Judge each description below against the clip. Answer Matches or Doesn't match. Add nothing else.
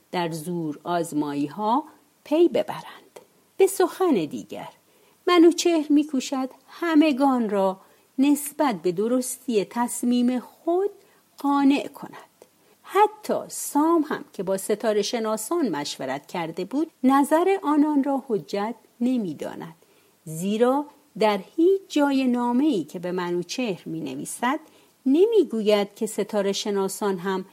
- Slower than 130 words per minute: Matches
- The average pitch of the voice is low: Doesn't match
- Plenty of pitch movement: Matches